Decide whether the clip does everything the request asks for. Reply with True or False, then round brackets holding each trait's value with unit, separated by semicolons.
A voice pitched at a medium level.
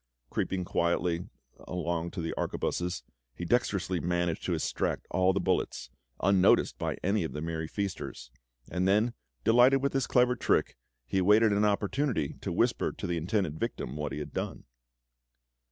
False (90 Hz)